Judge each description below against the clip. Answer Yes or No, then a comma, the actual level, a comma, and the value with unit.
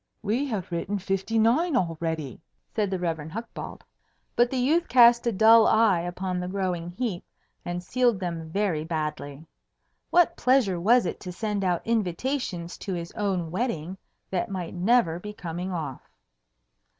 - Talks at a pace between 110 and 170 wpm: Yes, average, 155 wpm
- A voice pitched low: No, high, 190 Hz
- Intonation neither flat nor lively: Yes, average, 4.9 semitones